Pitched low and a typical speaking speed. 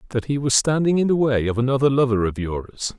No: low, 125 Hz; fast, 240 wpm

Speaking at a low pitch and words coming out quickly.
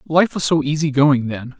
No: medium, 145 Hz; fast, 225 wpm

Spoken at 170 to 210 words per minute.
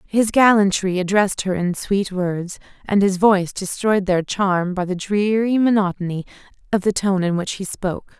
Yes: average, 175 wpm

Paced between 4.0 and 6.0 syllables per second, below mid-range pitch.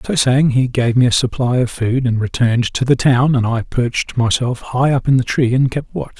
Yes: 5.2 syllables/s; low, 125 Hz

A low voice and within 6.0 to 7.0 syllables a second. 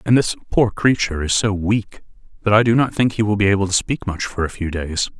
No: low, 105 Hz; 5.8 syllables/s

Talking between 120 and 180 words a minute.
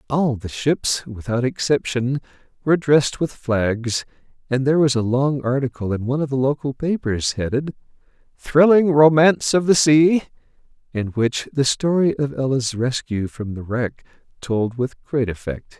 Yes: average, 155 wpm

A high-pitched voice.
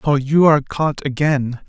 No: medium, 140 Hz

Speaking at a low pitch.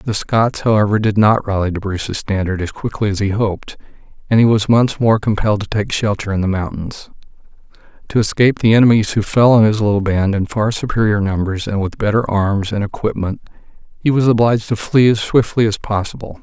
Yes: low, 105 Hz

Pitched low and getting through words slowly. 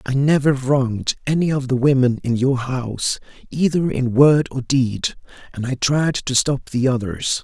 No: low, 130 Hz; average, 175 wpm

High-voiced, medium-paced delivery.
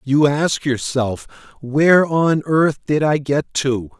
No: medium, 145 Hz; average, 150 wpm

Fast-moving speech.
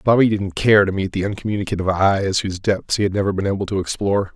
Yes: fast, 235 wpm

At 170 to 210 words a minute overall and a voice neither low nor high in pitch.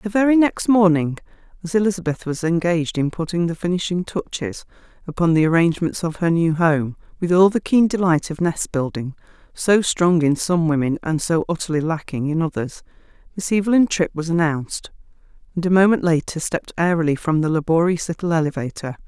Yes: average, 175 wpm; medium, 170 Hz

